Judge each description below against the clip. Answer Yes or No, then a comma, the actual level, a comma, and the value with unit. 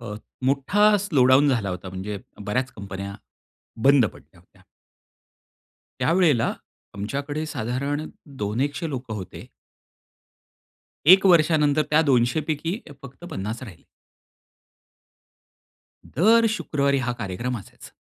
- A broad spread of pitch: Yes, wide, 6.1 semitones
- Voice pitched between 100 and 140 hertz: Yes, low, 135 Hz